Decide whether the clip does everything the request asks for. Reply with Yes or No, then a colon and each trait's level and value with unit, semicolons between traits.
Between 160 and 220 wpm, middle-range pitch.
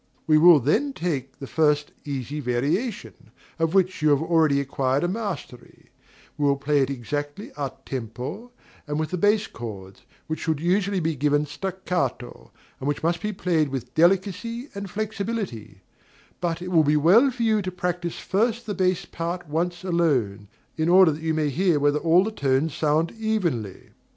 Yes: average, 175 wpm; medium, 160 Hz